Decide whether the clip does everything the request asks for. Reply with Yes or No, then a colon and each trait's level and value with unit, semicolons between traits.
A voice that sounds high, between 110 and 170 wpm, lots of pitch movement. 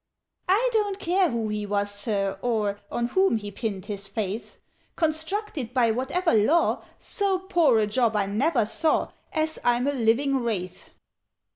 Yes: high, 240 Hz; average, 155 wpm; wide, 7.4 semitones